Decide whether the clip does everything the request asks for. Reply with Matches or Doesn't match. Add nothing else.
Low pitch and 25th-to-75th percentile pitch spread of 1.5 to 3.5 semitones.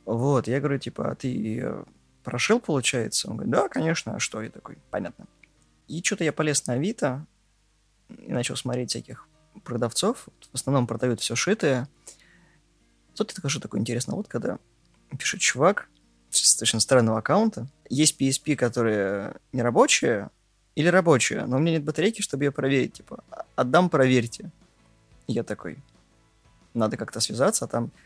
Doesn't match